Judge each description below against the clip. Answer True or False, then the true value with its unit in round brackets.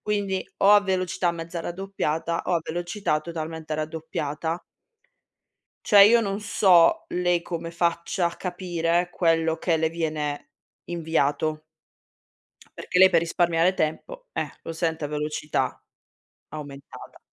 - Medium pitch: True (170 Hz)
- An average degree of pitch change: False (2.3 semitones)